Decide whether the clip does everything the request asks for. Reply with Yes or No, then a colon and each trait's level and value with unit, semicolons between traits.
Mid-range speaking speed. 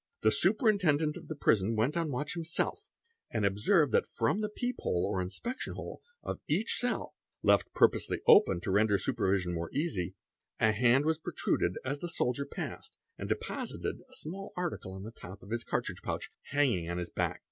Yes: average, 180 wpm